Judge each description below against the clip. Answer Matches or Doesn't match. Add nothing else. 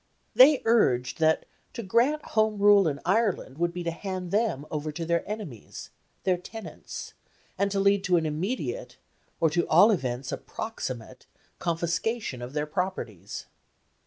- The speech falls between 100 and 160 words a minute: Matches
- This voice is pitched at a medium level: Matches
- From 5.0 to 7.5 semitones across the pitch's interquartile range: Matches